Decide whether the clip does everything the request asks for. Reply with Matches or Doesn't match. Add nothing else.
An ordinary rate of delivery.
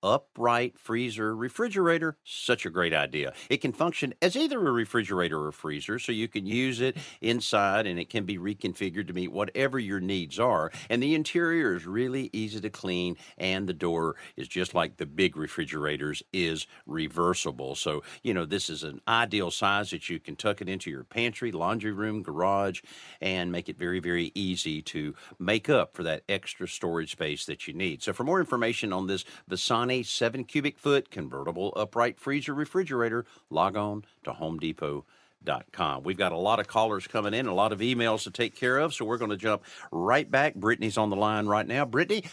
Matches